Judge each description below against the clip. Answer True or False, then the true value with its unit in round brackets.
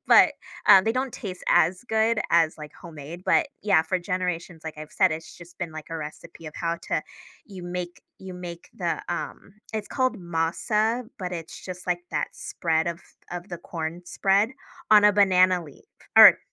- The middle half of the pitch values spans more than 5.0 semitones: False (2.9 semitones)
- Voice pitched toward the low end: False (175 Hz)